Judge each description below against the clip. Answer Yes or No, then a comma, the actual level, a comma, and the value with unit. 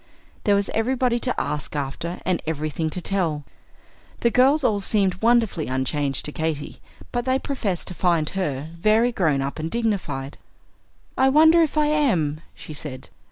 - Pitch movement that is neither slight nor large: No, wide, 8.0 semitones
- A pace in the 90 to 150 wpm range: No, average, 160 wpm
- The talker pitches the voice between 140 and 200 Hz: Yes, medium, 185 Hz